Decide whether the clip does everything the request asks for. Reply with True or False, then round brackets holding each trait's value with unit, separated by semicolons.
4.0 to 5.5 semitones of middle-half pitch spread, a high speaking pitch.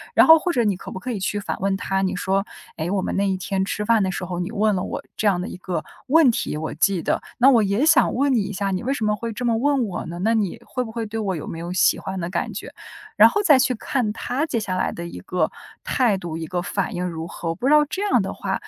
True (4.6 semitones; 200 Hz)